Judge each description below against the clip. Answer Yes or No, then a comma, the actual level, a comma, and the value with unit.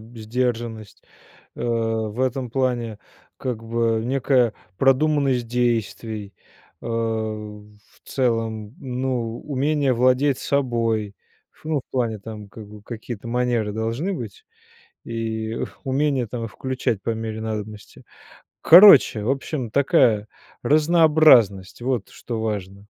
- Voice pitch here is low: Yes, low, 115 Hz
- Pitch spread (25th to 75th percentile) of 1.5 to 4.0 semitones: Yes, average, 2.9 semitones